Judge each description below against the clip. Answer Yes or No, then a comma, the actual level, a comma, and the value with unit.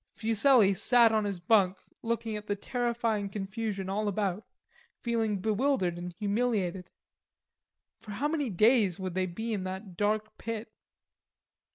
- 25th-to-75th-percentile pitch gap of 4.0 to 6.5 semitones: No, average, 3.0 semitones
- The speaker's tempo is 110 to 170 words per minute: Yes, average, 140 wpm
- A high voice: Yes, high, 210 Hz